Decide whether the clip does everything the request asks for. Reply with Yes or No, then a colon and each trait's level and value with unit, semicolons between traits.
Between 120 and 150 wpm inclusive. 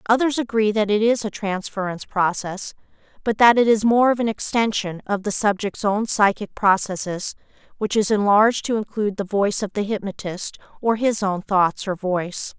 No: average, 180 wpm